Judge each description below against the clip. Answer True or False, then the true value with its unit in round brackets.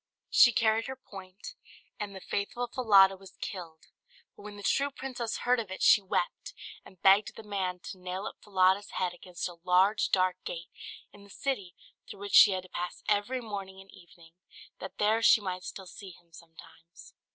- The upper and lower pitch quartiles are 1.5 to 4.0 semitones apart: True (2.5 semitones)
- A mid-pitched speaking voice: False (195 Hz)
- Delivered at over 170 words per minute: True (190 wpm)